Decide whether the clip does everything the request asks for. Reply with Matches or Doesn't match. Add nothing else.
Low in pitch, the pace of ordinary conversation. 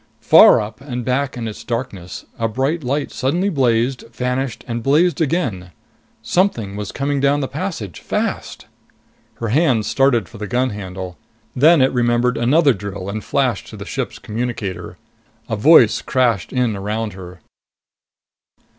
Matches